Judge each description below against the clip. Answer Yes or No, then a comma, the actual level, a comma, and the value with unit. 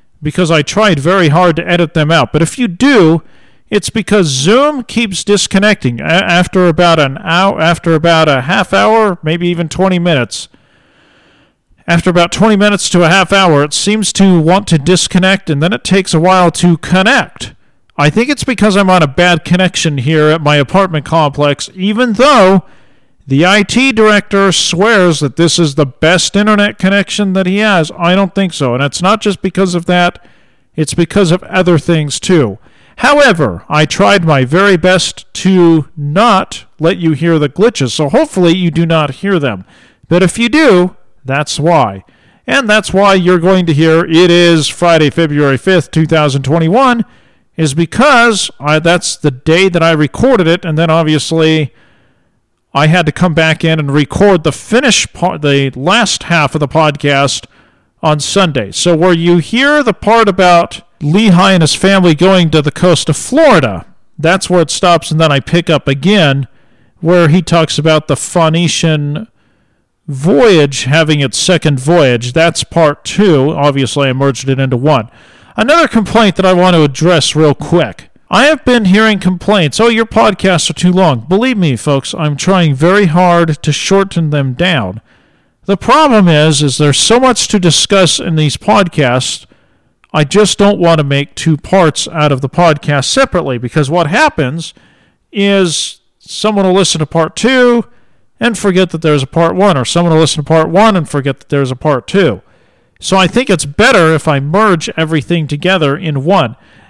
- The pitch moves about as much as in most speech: Yes, average, 4.2 semitones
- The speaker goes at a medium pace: Yes, average, 180 wpm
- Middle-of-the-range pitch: Yes, medium, 170 Hz